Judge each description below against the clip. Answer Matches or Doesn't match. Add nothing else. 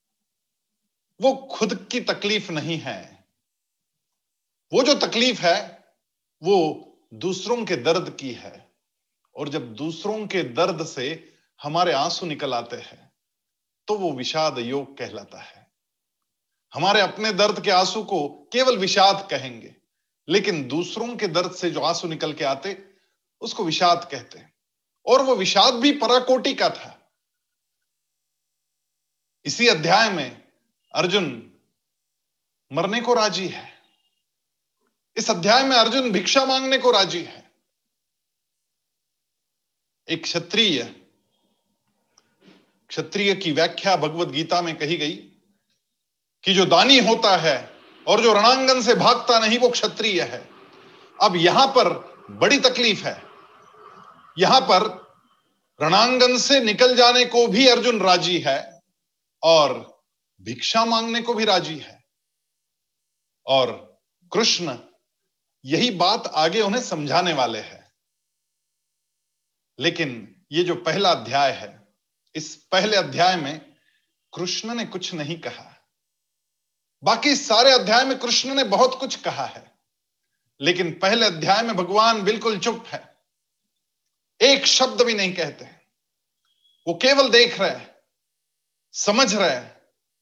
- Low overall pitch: Doesn't match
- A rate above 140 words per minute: Doesn't match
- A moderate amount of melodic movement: Doesn't match